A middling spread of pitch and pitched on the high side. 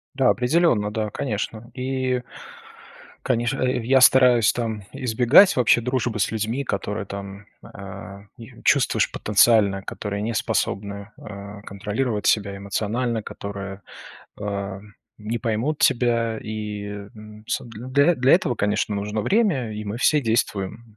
No: average, 3.3 semitones; low, 110 Hz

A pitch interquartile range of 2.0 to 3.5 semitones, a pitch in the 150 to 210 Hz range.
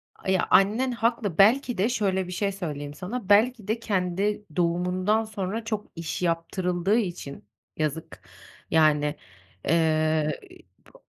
No: average, 4.4 semitones; high, 190 Hz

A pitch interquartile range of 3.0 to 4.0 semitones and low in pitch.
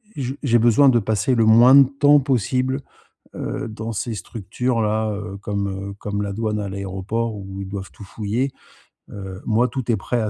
Yes: average, 3.6 semitones; low, 110 Hz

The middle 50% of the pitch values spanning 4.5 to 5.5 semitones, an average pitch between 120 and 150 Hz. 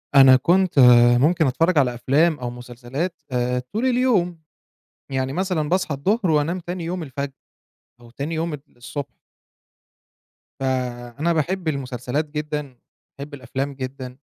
Yes: average, 4.9 semitones; medium, 140 Hz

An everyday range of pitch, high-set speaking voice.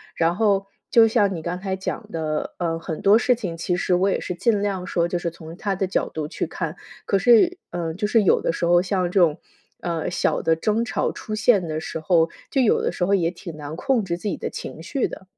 No: average, 3.7 semitones; medium, 180 Hz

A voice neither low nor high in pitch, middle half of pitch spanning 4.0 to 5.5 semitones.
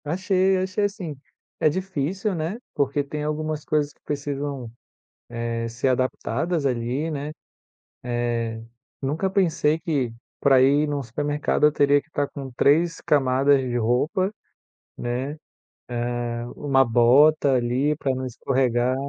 No: medium, 145 Hz; average, 3.3 semitones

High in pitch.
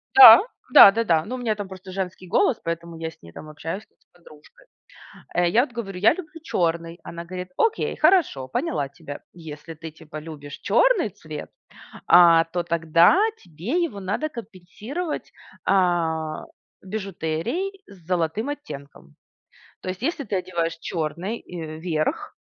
No: medium, 175 Hz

